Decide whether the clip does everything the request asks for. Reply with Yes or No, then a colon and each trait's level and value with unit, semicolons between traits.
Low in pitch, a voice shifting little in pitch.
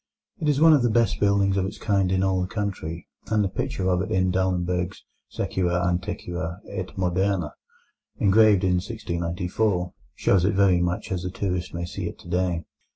Yes: very low, 95 Hz; narrow, 2.1 semitones